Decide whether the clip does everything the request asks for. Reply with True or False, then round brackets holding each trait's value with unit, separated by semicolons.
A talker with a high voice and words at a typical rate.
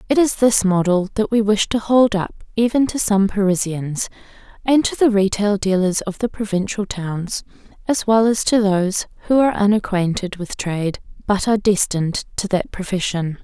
True (205 Hz; 175 wpm)